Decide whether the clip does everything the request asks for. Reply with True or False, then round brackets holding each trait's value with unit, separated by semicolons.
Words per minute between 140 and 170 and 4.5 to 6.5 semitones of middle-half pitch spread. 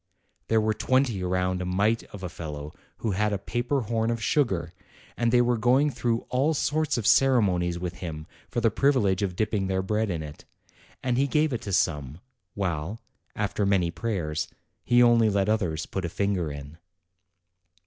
False (180 wpm; 4.9 semitones)